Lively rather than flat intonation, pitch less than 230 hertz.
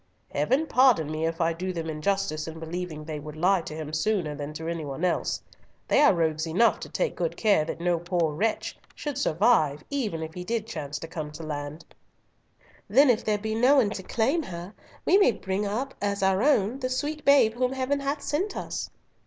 Yes: wide, 7.5 semitones; high, 190 Hz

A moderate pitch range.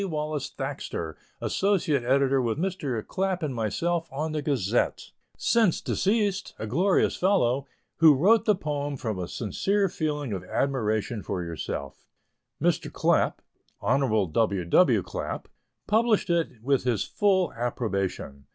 No: wide, 8.5 semitones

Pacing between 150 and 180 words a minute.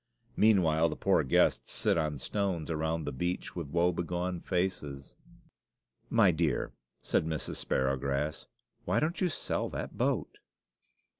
No: slow, 135 wpm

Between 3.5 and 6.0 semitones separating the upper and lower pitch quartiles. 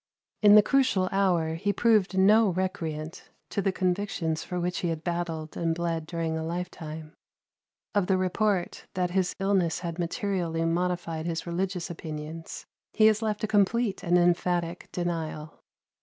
No: average, 2.8 semitones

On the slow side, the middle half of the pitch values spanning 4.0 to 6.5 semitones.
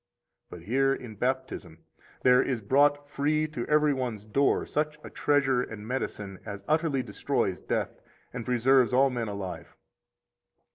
No: average, 145 wpm; average, 4.3 semitones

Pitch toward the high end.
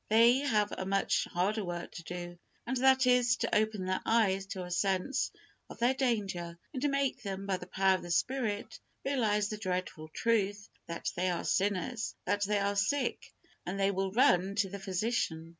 Yes: high, 200 Hz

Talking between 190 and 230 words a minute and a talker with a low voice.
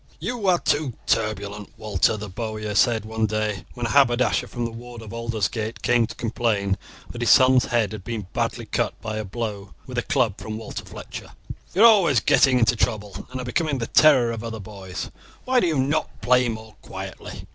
Yes: average, 200 wpm; low, 115 Hz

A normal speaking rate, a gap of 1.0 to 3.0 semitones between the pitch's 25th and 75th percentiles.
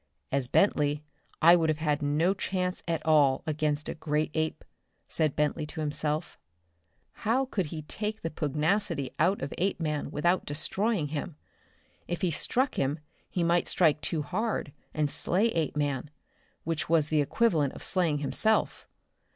No: average, 150 wpm; average, 3.4 semitones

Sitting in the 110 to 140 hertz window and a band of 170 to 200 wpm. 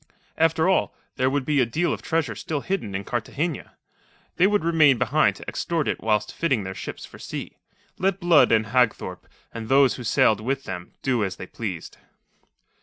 Yes: low, 135 Hz; average, 185 wpm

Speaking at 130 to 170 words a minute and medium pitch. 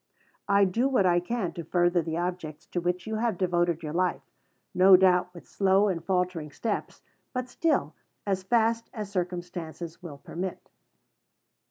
Yes: average, 165 wpm; medium, 180 Hz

